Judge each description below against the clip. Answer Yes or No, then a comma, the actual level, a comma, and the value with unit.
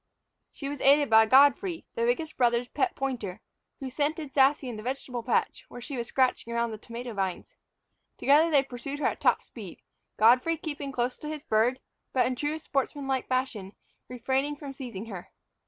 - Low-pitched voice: No, very high, 265 Hz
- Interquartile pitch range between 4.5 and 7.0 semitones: No, average, 3.5 semitones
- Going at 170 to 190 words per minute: Yes, average, 180 wpm